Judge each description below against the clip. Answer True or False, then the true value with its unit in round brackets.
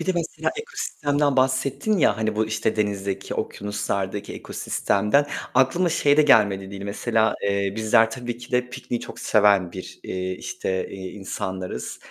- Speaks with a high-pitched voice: False (110 Hz)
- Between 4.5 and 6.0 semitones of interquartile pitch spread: True (4.8 semitones)